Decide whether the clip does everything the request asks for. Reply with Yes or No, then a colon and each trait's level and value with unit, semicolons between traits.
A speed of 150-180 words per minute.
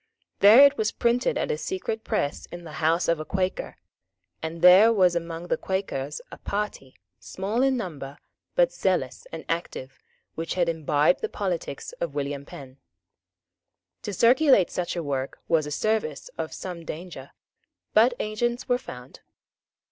Yes: average, 155 wpm